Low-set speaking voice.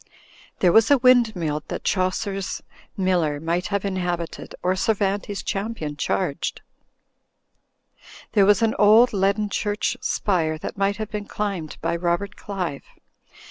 No: high, 195 Hz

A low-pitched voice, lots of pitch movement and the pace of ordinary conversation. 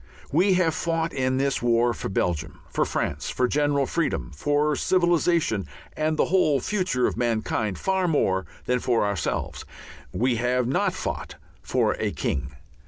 Yes: low, 130 Hz; wide, 5.8 semitones; average, 155 wpm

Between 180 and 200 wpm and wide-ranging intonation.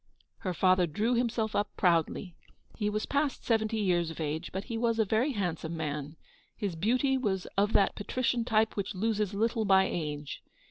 No: average, 185 wpm; average, 4.3 semitones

